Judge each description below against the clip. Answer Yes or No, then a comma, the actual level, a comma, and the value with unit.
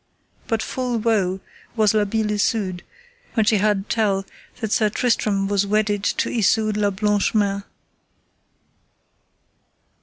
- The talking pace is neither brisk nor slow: No, slow, 125 wpm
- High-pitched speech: Yes, high, 210 Hz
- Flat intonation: Yes, narrow, 1.7 semitones